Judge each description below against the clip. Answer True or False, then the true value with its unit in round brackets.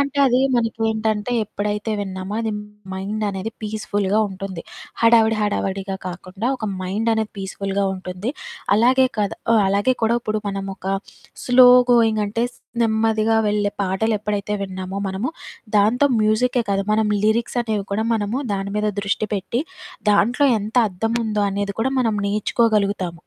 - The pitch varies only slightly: True (2.2 semitones)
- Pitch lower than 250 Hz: True (210 Hz)